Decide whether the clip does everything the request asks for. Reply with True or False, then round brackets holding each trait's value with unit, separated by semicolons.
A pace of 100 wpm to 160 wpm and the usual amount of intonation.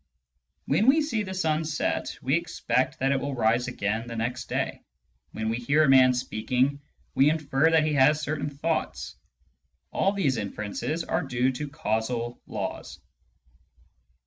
True (155 wpm; 4.2 semitones)